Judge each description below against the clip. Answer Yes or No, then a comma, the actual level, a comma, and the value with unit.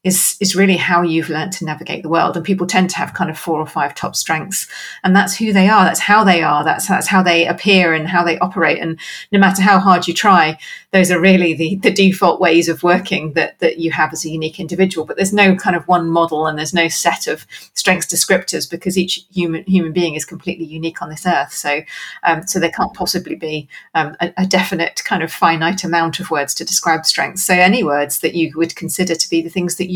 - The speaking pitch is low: No, medium, 175 Hz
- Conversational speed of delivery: No, fast, 240 wpm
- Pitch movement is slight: Yes, narrow, 2.2 semitones